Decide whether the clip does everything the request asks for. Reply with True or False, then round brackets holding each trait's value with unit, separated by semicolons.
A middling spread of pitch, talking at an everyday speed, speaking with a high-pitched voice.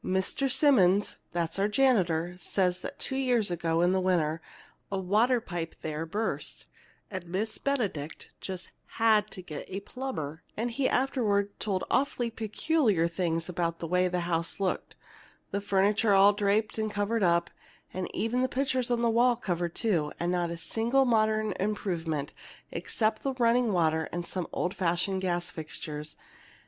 True (4.7 semitones; 160 wpm; 195 Hz)